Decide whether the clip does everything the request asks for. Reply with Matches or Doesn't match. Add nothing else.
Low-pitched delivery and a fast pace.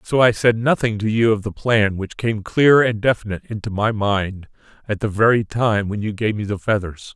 Matches